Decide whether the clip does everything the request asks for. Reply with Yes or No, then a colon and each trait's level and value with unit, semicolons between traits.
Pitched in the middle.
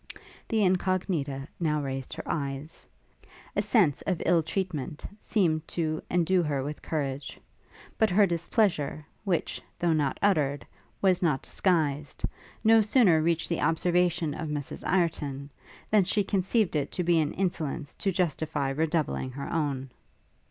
Yes: medium, 160 Hz